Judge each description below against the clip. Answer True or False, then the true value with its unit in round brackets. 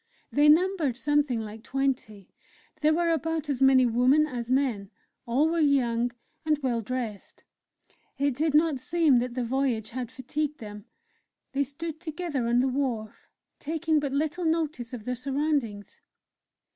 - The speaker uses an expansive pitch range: False (4.1 semitones)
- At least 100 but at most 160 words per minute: True (150 wpm)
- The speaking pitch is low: False (270 Hz)